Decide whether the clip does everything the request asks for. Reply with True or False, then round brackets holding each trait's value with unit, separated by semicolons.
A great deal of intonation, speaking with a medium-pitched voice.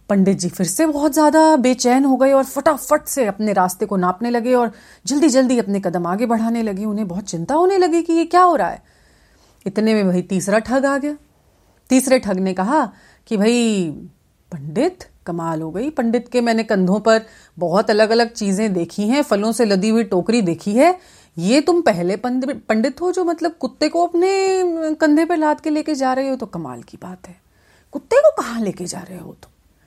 False (7.4 semitones; 235 Hz)